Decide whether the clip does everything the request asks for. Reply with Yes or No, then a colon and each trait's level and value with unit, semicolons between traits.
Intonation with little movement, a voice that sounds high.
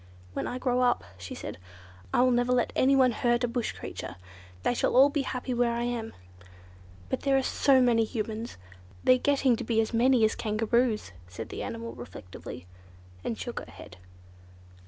Yes: narrow, 2.2 semitones; high, 240 Hz